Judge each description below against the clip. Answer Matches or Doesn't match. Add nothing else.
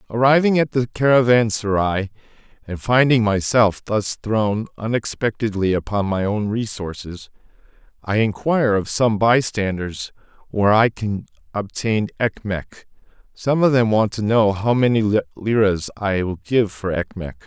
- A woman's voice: Doesn't match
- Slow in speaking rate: Matches